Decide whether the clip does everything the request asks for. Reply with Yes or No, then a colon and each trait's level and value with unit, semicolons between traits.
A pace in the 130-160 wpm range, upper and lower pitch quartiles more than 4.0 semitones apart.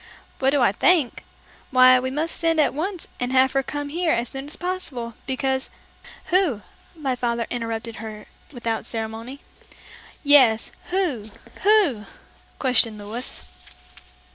Yes: average, 140 wpm; average, 4.5 semitones